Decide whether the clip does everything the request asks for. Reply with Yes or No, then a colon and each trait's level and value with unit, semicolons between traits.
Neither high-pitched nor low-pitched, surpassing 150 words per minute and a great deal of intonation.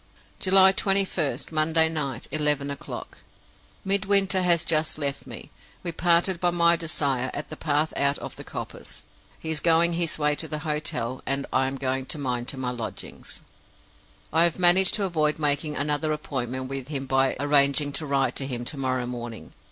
No: medium, 150 Hz; average, 170 wpm; average, 3.8 semitones